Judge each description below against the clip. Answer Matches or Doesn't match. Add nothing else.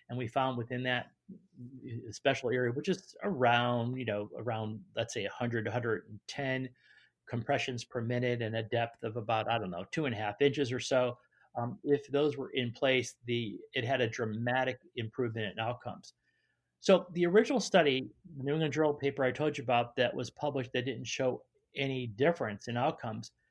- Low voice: Matches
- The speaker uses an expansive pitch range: Doesn't match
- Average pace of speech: Matches